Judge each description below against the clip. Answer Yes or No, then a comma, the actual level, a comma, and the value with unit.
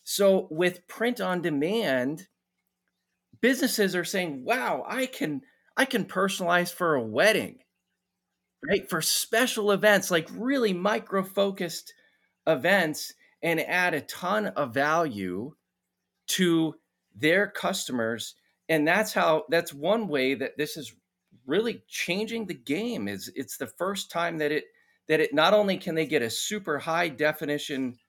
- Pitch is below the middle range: No, medium, 180 Hz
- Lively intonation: Yes, wide, 5.7 semitones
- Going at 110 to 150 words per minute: Yes, average, 140 wpm